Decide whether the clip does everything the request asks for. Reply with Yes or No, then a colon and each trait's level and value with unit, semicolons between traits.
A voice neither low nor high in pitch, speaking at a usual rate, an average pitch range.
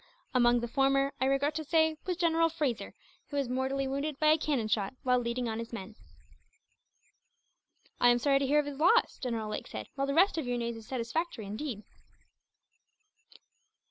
No: very high, 270 Hz; average, 185 wpm; average, 4.0 semitones